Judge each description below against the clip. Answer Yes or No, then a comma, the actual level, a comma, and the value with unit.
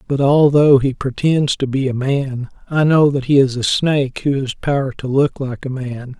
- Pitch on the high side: No, low, 135 Hz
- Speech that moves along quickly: Yes, fast, 225 wpm